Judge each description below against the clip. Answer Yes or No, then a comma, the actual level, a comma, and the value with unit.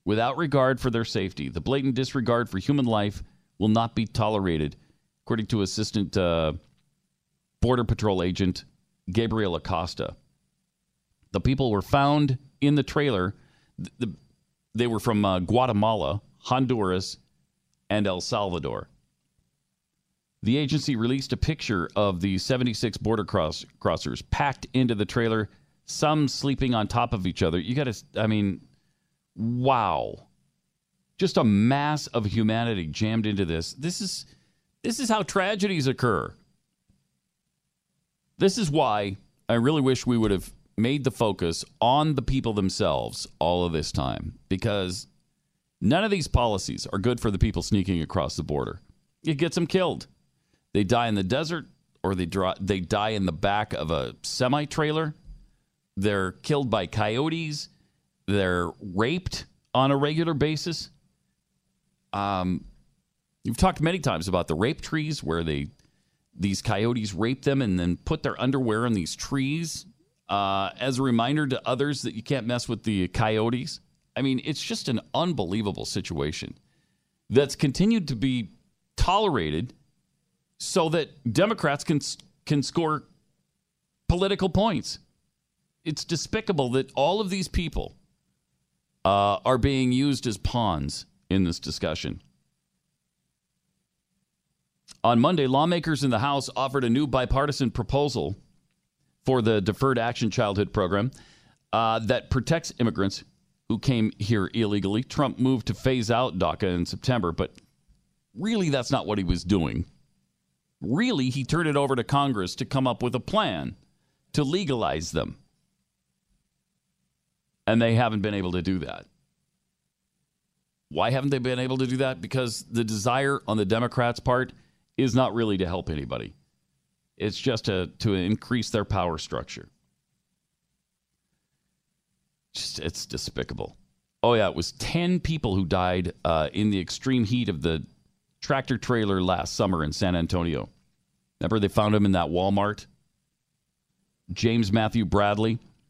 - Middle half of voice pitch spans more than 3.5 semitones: Yes, wide, 5.6 semitones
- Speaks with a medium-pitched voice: No, low, 115 Hz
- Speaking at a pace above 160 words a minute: No, average, 145 wpm